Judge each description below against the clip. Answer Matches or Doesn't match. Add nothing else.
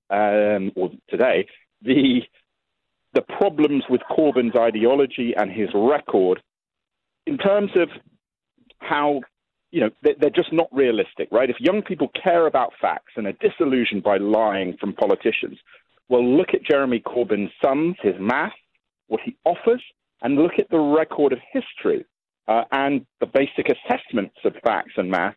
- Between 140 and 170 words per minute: Matches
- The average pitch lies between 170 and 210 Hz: Doesn't match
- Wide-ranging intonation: Matches